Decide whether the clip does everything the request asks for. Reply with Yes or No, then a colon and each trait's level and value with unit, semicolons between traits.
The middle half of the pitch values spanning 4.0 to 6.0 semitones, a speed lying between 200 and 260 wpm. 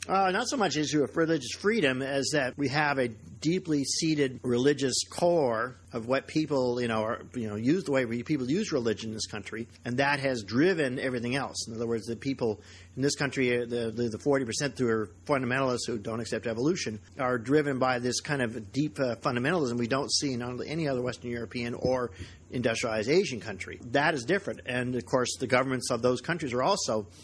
No: average, 3.3 semitones; fast, 205 wpm